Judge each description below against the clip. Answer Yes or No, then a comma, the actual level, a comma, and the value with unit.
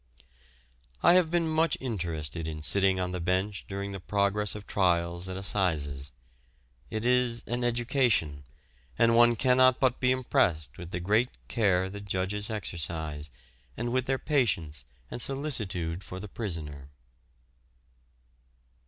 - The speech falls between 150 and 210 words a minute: No, slow, 135 wpm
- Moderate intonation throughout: No, wide, 5.9 semitones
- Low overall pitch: Yes, low, 100 Hz